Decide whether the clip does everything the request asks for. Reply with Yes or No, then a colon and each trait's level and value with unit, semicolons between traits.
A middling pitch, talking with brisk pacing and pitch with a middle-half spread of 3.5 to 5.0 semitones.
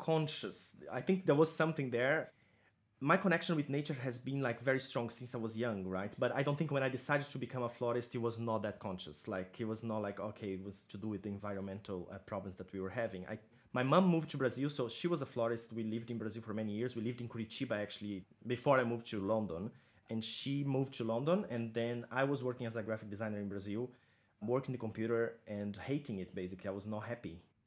No: low, 115 Hz; fast, 240 wpm; average, 3.8 semitones